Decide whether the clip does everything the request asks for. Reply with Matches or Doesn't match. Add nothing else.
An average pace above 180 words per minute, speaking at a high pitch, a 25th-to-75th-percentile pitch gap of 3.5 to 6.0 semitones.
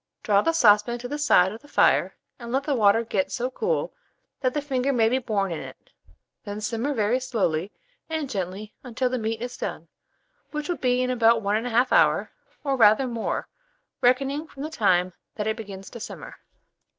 Matches